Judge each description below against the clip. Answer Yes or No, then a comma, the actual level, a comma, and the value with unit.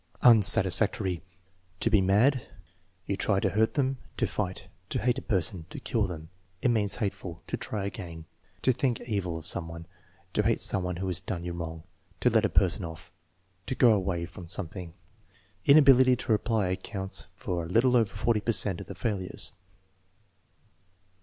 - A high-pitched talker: No, low, 100 Hz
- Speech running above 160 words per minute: Yes, average, 180 wpm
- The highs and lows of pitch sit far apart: No, average, 4.6 semitones